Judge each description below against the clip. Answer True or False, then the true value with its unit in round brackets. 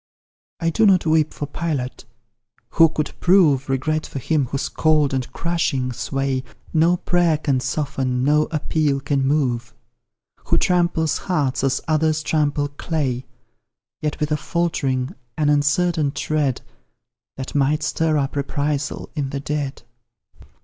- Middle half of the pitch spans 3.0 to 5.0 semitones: False (2.6 semitones)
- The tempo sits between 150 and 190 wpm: False (135 wpm)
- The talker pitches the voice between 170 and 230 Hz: False (150 Hz)